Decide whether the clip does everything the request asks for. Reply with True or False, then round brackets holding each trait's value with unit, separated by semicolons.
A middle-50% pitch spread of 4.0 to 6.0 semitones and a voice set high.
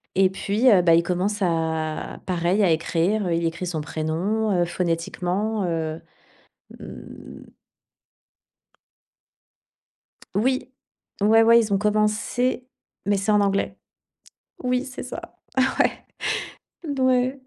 True (4.5 semitones; 195 Hz)